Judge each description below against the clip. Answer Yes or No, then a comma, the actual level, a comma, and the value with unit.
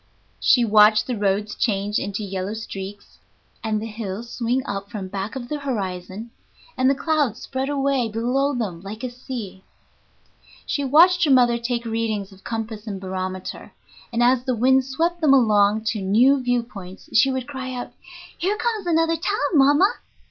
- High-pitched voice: Yes, high, 235 Hz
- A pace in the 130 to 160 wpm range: No, average, 170 wpm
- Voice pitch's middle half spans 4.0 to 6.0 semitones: Yes, average, 4.6 semitones